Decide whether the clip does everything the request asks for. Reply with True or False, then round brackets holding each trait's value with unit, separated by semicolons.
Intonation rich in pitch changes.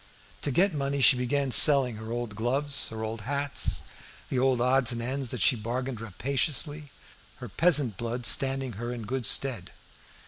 False (2.9 semitones)